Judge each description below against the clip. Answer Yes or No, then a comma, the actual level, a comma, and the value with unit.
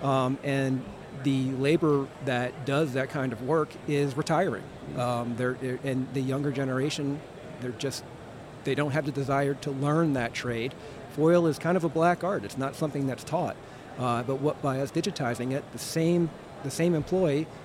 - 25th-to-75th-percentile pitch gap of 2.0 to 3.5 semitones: Yes, average, 2.9 semitones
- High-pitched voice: No, medium, 140 Hz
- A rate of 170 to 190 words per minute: Yes, average, 185 wpm